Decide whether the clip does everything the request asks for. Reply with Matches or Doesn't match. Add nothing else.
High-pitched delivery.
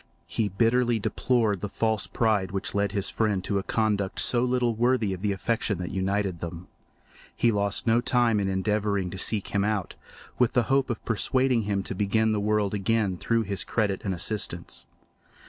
Doesn't match